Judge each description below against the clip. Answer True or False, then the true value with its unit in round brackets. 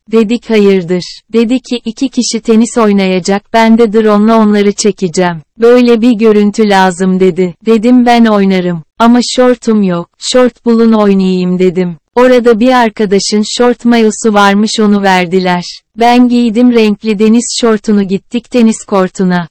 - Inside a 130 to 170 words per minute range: True (135 wpm)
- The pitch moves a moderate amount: True (3.6 semitones)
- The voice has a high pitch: True (220 Hz)